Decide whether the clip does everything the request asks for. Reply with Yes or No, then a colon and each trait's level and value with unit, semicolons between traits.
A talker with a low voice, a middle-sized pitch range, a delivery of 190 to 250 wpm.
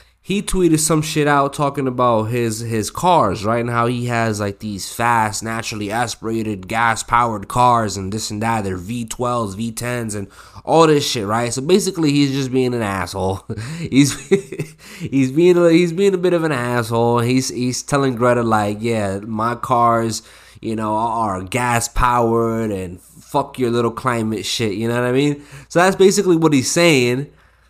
No: low, 120 Hz; average, 4.1 semitones; average, 180 wpm